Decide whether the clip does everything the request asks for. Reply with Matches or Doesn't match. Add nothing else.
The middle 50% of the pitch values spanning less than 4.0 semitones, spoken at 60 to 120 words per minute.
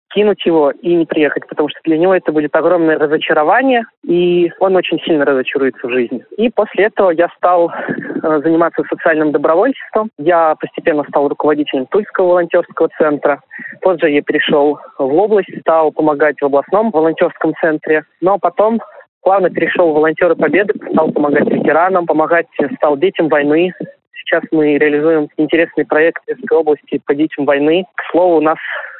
Doesn't match